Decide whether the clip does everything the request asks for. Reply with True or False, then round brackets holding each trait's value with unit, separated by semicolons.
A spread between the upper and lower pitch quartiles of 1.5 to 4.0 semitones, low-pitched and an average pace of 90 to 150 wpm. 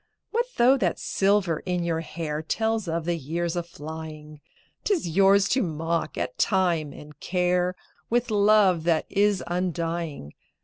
False (3.6 semitones; 175 Hz; 145 wpm)